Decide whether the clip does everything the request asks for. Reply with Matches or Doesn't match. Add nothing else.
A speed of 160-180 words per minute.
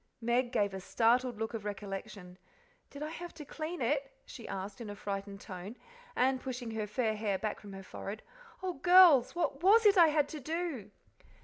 Doesn't match